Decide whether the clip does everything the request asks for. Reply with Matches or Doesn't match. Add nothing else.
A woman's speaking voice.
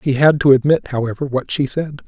Doesn't match